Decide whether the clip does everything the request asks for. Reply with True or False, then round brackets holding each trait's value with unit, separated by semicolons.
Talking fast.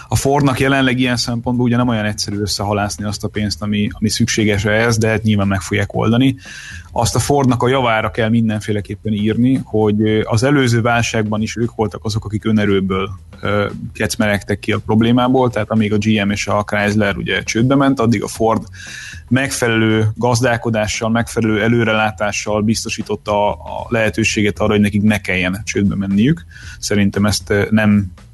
True (160 wpm)